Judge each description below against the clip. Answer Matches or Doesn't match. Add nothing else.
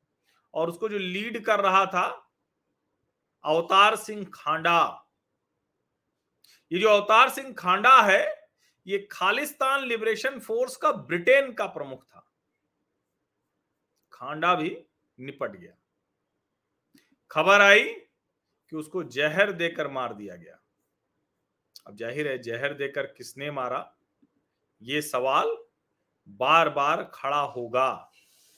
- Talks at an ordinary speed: Doesn't match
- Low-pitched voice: Doesn't match